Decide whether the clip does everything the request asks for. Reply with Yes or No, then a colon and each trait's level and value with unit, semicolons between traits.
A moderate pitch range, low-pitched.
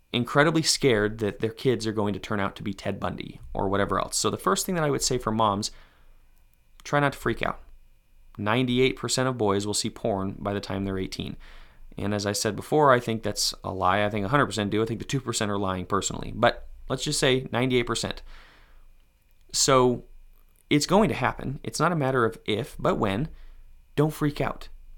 Yes: average, 4.7 semitones; low, 110 Hz